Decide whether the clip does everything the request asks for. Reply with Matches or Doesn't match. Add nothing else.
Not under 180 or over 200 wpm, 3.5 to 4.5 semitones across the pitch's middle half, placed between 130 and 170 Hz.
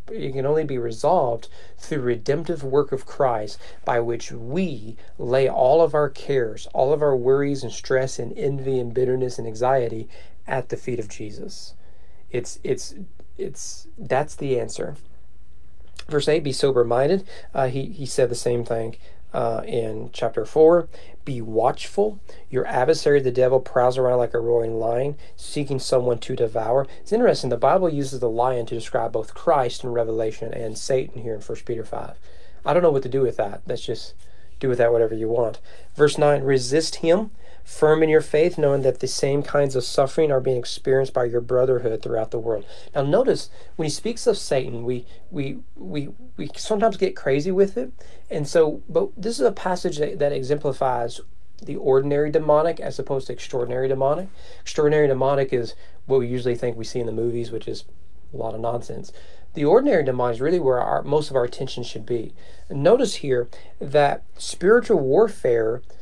Matches